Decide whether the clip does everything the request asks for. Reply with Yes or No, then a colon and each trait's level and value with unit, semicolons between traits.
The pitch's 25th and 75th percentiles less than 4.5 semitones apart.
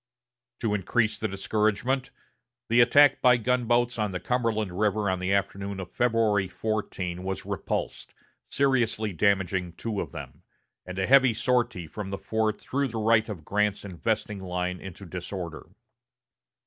Yes: average, 3.5 semitones